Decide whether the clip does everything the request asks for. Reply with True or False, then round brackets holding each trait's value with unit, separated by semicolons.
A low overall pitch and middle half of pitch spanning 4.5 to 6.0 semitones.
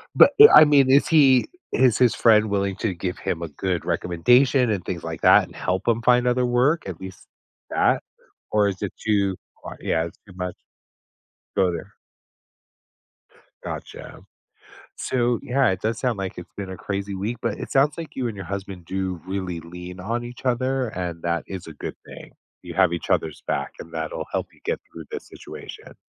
True (100 Hz; 5.3 semitones)